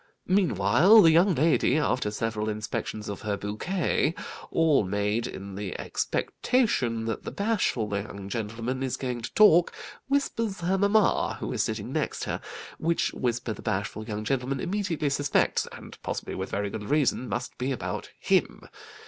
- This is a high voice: No, low, 125 Hz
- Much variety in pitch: Yes, wide, 8.0 semitones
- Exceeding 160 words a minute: No, average, 155 wpm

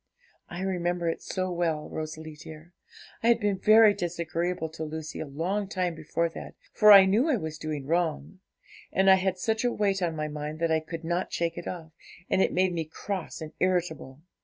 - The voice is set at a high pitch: No, medium, 170 Hz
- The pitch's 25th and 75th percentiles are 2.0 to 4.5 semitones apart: Yes, average, 3.2 semitones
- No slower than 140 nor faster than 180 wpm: No, fast, 205 wpm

